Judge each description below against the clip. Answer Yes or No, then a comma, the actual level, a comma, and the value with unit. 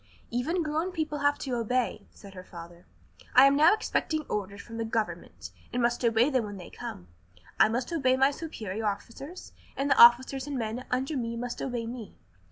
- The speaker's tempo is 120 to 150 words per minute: No, average, 190 wpm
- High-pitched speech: Yes, high, 245 Hz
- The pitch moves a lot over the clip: No, average, 4.1 semitones